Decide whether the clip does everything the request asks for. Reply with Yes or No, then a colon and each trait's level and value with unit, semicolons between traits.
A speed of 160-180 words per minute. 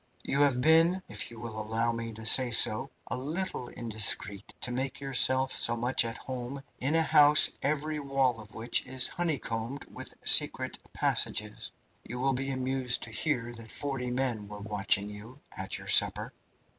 Yes: average, 170 wpm